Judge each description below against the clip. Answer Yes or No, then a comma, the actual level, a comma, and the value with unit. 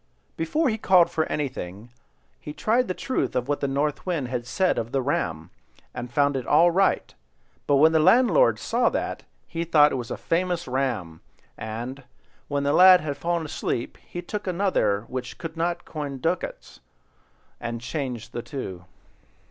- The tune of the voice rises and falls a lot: Yes, wide, 5.8 semitones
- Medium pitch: Yes, medium, 145 Hz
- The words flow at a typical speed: Yes, average, 170 wpm